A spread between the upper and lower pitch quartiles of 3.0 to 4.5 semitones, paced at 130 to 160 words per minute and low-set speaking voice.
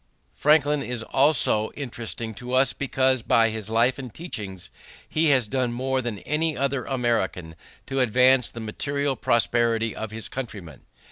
Yes: average, 3.3 semitones; average, 150 wpm; low, 125 Hz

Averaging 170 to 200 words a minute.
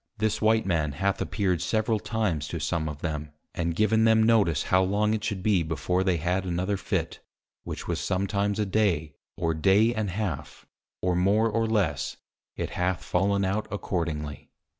Yes: average, 175 wpm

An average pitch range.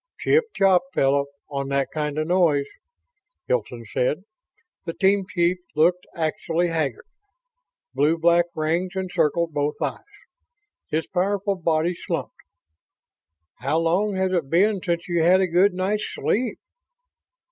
Yes: average, 3.3 semitones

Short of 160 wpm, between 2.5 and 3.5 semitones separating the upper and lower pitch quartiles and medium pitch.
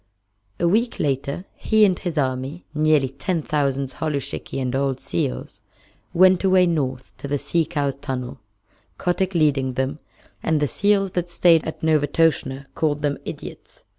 No: average, 150 wpm; average, 4.2 semitones; medium, 150 Hz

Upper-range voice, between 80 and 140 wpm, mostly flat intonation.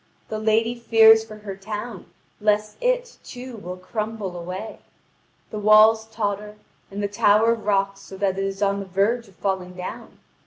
No: high, 210 Hz; average, 165 wpm; narrow, 2.1 semitones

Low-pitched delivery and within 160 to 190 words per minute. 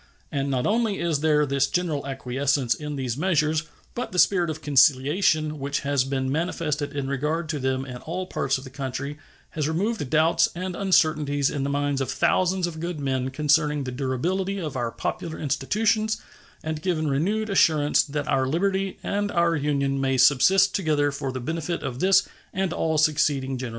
No: medium, 150 Hz; average, 180 wpm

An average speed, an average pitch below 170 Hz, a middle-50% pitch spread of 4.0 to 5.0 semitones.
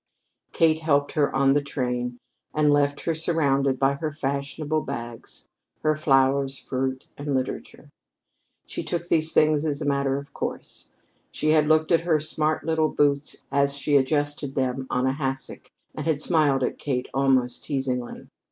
No: average, 160 wpm; medium, 140 Hz; narrow, 2.4 semitones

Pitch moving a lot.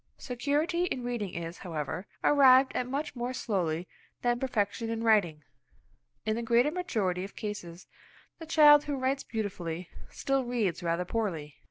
Yes: wide, 6.6 semitones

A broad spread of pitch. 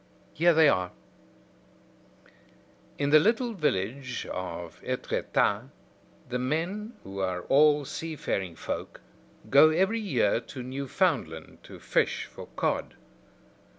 Yes: wide, 8.9 semitones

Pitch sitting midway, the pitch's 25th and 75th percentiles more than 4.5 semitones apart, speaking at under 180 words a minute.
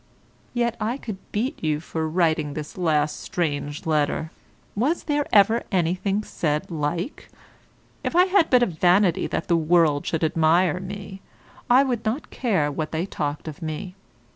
Yes: medium, 175 Hz; wide, 5.6 semitones; average, 160 wpm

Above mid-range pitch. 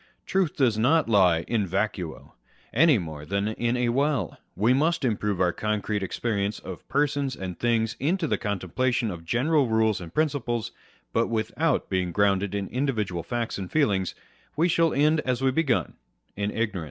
No: low, 115 Hz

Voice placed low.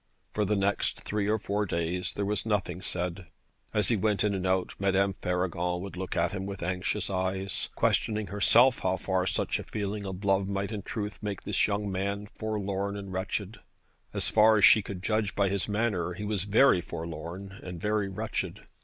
Yes: low, 100 Hz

